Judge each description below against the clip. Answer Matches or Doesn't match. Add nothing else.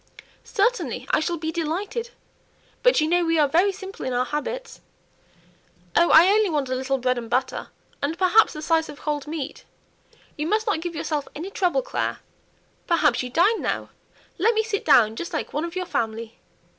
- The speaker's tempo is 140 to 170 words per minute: Doesn't match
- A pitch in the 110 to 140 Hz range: Doesn't match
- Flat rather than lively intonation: Doesn't match